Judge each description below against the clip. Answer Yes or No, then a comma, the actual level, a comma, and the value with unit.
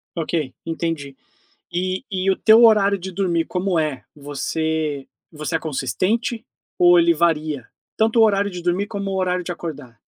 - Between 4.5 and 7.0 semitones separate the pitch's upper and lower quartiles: No, average, 3.9 semitones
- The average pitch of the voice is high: No, medium, 175 Hz